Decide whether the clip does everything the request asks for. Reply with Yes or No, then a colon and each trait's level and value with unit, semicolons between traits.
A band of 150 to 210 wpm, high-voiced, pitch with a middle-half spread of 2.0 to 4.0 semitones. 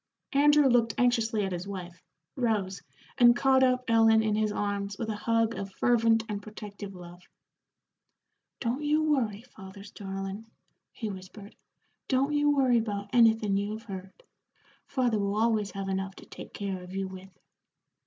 Yes: average, 160 wpm; high, 215 Hz; average, 3.4 semitones